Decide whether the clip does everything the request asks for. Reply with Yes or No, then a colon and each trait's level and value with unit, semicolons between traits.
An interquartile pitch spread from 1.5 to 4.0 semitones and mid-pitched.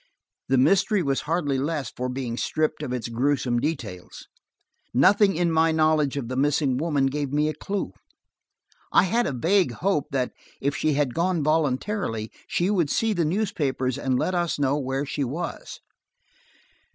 No: average, 4.4 semitones; medium, 145 Hz